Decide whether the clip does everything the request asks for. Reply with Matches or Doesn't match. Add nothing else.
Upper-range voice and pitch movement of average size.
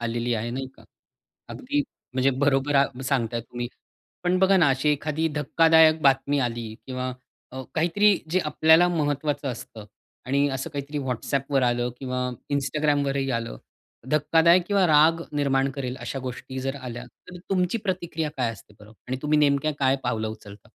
Doesn't match